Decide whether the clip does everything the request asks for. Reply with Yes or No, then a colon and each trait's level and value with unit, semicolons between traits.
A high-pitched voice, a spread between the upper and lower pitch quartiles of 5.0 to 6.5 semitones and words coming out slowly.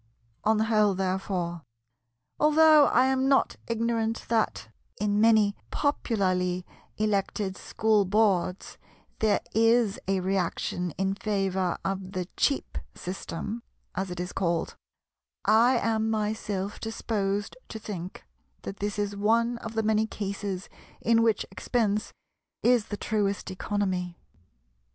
No: high, 205 Hz; average, 3.0 semitones; slow, 120 wpm